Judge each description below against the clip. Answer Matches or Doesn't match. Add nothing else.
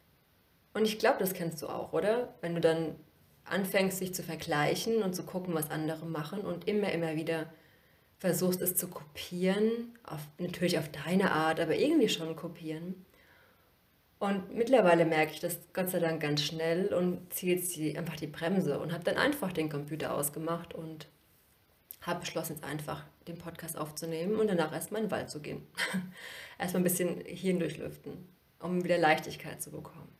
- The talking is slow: Doesn't match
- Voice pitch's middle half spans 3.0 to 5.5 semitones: Doesn't match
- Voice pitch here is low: Doesn't match